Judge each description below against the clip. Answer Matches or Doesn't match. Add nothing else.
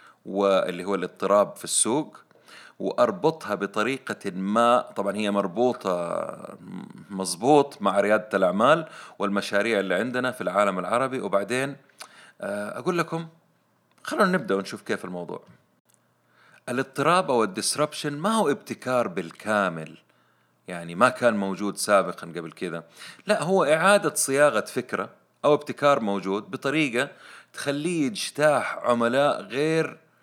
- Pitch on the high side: Doesn't match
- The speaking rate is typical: Matches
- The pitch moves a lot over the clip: Matches